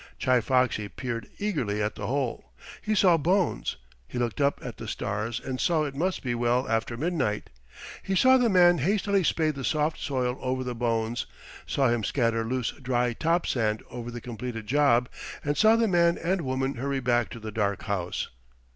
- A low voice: Yes, low, 130 Hz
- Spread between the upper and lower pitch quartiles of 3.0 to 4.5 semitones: No, wide, 5.5 semitones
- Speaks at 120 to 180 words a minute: No, average, 190 wpm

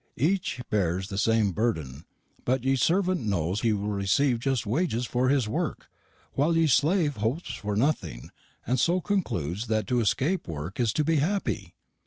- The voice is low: Yes, low, 120 Hz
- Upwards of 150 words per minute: Yes, average, 170 wpm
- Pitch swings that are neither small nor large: No, wide, 6.6 semitones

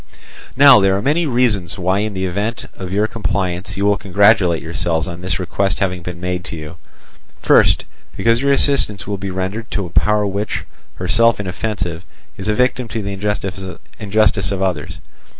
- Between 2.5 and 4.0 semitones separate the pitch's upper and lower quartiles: Yes, average, 2.9 semitones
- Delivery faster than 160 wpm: Yes, average, 175 wpm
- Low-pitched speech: Yes, low, 100 Hz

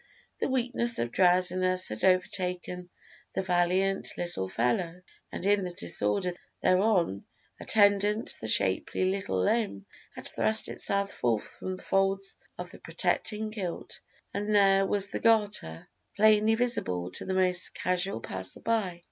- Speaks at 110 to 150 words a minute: Yes, average, 140 wpm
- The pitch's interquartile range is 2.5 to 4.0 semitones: Yes, average, 2.8 semitones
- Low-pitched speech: No, medium, 185 Hz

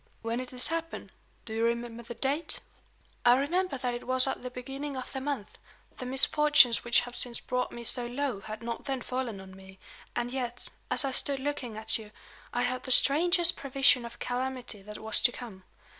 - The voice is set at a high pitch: Yes, very high, 250 Hz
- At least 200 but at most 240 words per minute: Yes, fast, 205 wpm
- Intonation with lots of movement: No, narrow, 2.5 semitones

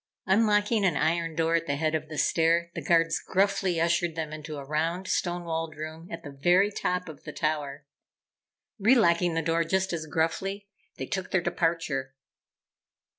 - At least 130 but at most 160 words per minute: No, average, 175 wpm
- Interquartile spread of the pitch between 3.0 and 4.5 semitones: No, narrow, 2.5 semitones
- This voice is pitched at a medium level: Yes, medium, 165 Hz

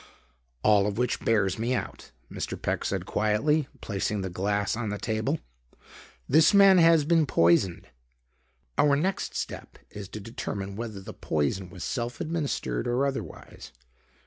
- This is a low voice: Yes, low, 110 Hz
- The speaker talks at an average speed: Yes, average, 145 wpm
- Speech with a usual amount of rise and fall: No, wide, 6.1 semitones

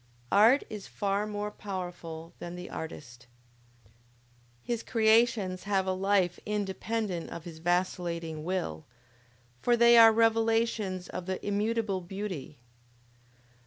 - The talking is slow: Yes, slow, 115 wpm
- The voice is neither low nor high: No, high, 195 Hz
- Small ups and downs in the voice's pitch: No, average, 3.7 semitones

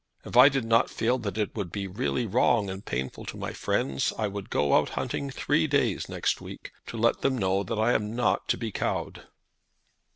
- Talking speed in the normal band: No, fast, 215 wpm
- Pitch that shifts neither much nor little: Yes, average, 4.0 semitones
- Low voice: Yes, low, 110 Hz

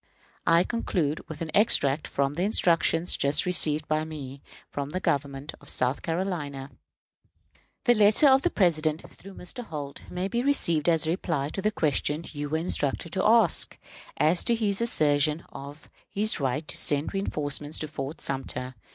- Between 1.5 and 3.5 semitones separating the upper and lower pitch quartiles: No, average, 4.3 semitones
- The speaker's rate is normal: Yes, average, 170 wpm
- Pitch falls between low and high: Yes, medium, 155 Hz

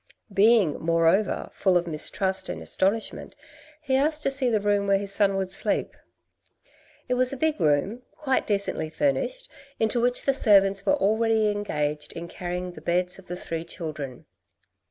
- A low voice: No, high, 200 Hz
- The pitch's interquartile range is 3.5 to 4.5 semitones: No, average, 5.2 semitones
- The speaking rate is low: No, average, 165 wpm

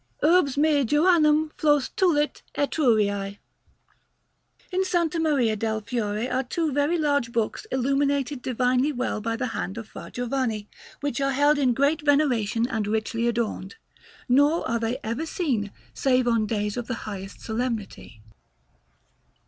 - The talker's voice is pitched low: No, very high, 255 Hz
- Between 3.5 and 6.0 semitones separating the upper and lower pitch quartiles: Yes, average, 4.5 semitones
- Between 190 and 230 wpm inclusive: No, average, 140 wpm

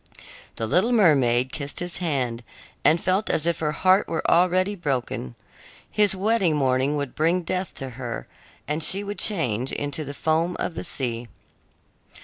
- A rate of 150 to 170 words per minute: Yes, average, 160 wpm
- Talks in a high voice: No, medium, 160 Hz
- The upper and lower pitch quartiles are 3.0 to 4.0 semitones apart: No, wide, 5.6 semitones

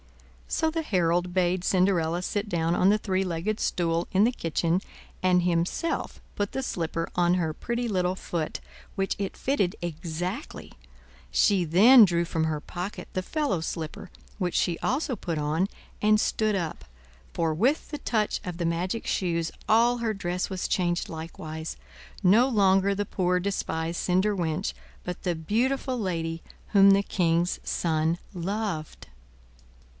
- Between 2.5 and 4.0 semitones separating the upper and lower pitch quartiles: Yes, average, 3.6 semitones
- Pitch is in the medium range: Yes, medium, 180 Hz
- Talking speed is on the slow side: No, average, 150 wpm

